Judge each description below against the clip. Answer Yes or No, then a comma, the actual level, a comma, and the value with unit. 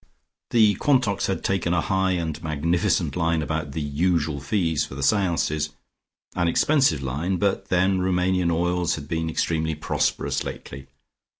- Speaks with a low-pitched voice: Yes, very low, 85 Hz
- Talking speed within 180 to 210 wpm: No, average, 145 wpm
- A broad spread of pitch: No, average, 3.2 semitones